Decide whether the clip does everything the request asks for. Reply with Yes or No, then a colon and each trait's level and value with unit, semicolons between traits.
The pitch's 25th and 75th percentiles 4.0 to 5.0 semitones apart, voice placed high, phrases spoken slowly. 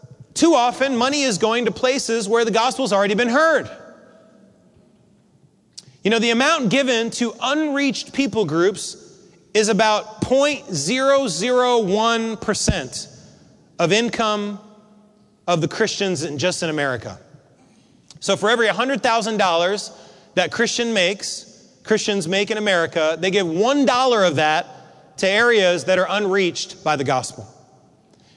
Yes: average, 4.6 semitones; high, 215 Hz; slow, 125 wpm